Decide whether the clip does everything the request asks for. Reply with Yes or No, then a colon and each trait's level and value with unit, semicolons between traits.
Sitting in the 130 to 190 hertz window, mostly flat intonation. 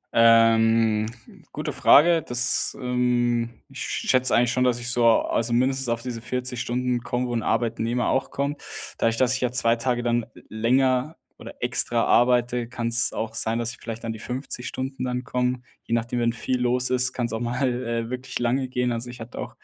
No: low, 120 Hz; narrow, 1.4 semitones